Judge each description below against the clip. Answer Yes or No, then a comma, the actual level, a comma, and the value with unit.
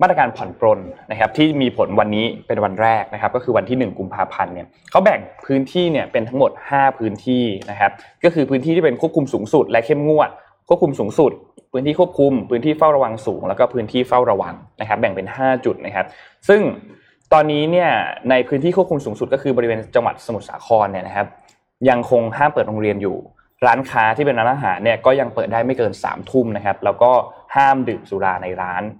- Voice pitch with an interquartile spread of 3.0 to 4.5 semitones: No, average, 5.2 semitones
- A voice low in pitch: Yes, low, 125 Hz